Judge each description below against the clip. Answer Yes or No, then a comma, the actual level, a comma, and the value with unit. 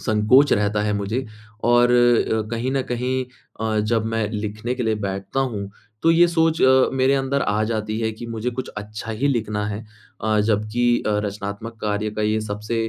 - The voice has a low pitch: Yes, low, 110 Hz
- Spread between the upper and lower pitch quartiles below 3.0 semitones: Yes, narrow, 2.6 semitones